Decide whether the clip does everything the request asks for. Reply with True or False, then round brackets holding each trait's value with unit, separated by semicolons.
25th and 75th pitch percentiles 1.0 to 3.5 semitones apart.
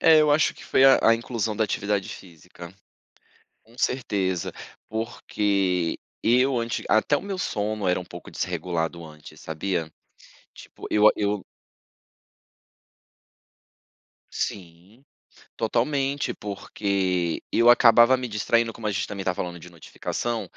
False (4.7 semitones)